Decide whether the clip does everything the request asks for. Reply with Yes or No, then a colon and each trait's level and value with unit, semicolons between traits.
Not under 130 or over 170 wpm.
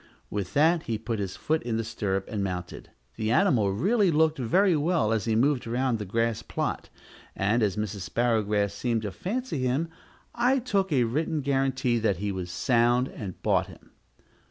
No: average, 180 wpm